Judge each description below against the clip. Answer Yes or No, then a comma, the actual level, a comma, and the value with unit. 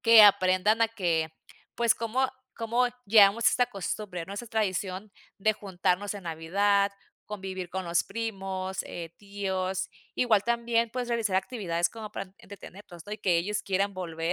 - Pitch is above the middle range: Yes, high, 200 Hz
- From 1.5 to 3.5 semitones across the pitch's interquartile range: Yes, average, 3.1 semitones